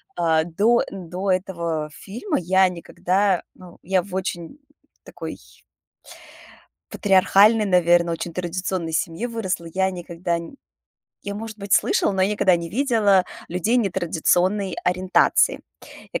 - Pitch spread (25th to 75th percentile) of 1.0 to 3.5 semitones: Yes, average, 2.7 semitones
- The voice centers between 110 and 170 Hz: No, medium, 185 Hz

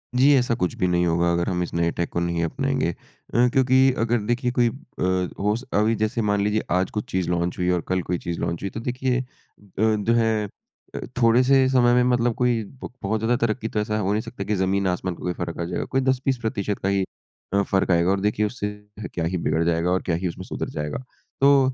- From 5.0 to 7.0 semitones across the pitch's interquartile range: Yes, wide, 5.4 semitones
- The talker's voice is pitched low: Yes, low, 105 Hz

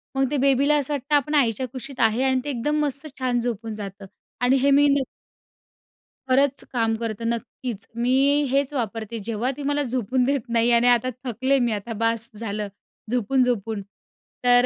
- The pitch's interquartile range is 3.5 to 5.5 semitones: No, average, 3.0 semitones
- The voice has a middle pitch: No, high, 245 Hz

